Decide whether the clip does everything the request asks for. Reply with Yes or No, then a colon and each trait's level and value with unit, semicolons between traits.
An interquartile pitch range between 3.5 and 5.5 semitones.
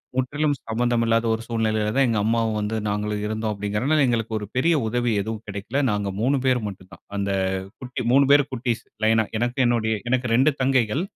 No: average, 3.0 semitones